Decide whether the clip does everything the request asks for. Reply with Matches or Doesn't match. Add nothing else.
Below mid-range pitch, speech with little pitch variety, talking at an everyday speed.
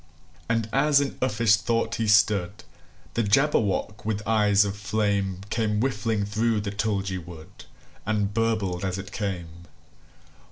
Doesn't match